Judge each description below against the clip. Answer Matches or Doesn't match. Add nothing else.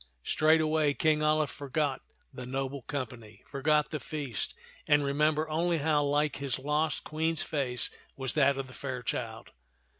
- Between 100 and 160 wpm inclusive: Matches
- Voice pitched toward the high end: Doesn't match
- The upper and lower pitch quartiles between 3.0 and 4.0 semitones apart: Doesn't match